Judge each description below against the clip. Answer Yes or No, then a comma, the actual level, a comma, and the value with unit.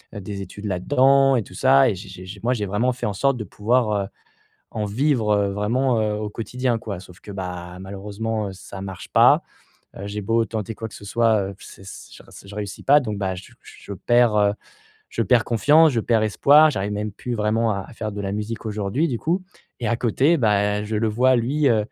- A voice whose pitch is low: Yes, low, 105 Hz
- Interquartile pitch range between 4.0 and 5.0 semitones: No, average, 3.2 semitones